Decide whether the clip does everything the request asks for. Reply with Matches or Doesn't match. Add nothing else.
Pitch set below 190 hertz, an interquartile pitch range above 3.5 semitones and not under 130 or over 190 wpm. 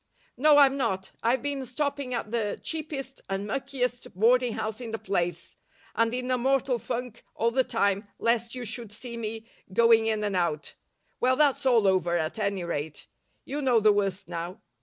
Doesn't match